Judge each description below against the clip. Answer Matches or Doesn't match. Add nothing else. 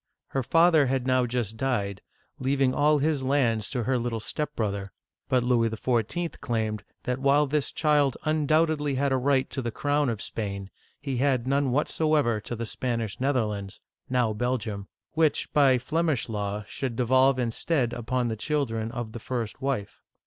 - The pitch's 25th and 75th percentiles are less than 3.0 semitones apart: Doesn't match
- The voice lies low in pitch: Matches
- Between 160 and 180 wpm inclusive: Matches